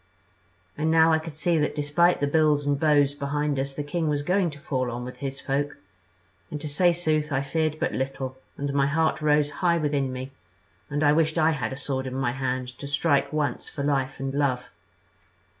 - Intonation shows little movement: Yes, narrow, 2.3 semitones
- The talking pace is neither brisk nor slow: No, fast, 210 wpm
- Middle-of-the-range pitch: Yes, medium, 145 Hz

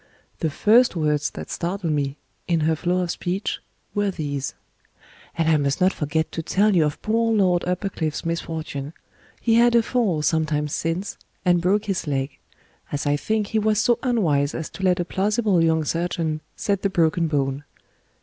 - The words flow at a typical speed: Yes, average, 180 wpm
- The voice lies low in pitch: No, medium, 170 Hz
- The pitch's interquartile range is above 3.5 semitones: Yes, average, 4.7 semitones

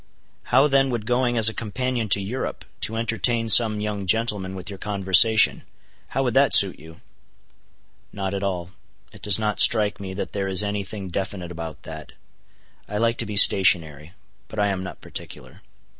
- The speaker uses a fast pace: No, average, 175 wpm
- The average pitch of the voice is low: Yes, low, 105 Hz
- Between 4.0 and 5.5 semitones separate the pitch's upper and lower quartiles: No, average, 3.0 semitones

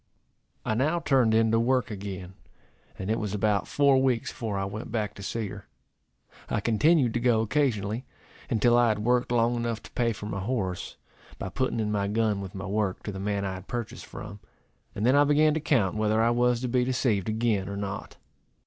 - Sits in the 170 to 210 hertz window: No, low, 110 Hz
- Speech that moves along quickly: Yes, fast, 210 wpm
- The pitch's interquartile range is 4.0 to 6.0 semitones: No, average, 3.2 semitones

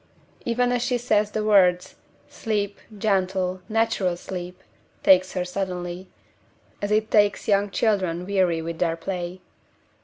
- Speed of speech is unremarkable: No, slow, 130 wpm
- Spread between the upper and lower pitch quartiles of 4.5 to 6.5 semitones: No, average, 2.7 semitones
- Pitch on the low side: No, high, 190 Hz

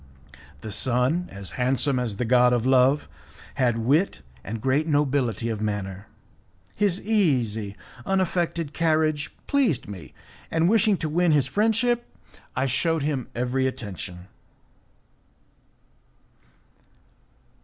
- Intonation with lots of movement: Yes, wide, 6.2 semitones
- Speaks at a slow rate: Yes, slow, 110 wpm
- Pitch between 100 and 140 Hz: Yes, low, 135 Hz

